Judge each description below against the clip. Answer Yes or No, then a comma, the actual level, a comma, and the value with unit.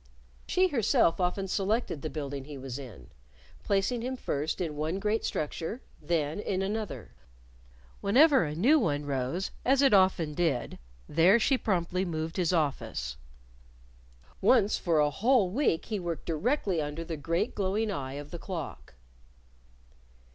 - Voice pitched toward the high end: No, medium, 175 Hz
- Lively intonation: Yes, wide, 5.9 semitones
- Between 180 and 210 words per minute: No, average, 145 wpm